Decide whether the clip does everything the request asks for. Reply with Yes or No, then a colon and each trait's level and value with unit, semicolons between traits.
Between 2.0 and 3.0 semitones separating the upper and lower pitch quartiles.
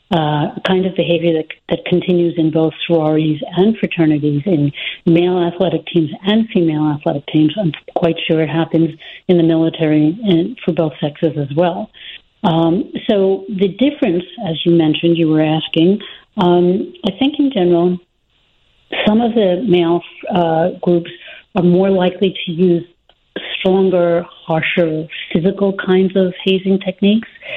Yes: average, 2.7 semitones